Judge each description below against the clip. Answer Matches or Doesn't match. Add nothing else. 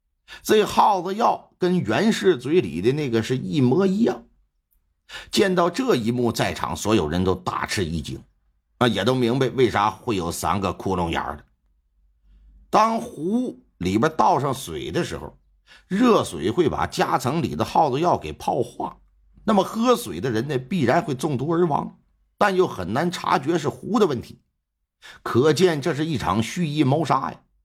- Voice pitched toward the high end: Doesn't match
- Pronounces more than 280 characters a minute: Doesn't match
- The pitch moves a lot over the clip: Matches